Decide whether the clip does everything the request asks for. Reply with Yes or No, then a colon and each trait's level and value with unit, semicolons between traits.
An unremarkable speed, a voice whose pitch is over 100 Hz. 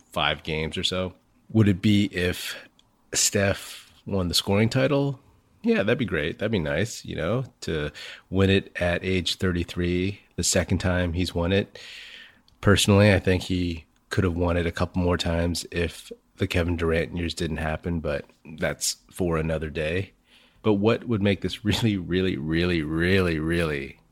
No: average, 170 wpm; very low, 90 Hz